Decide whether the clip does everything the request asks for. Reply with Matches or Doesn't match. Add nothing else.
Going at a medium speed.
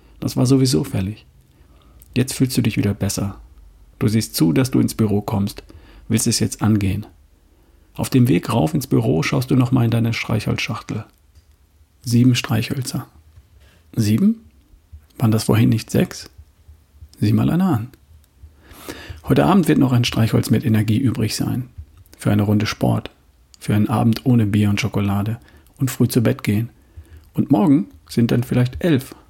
Matches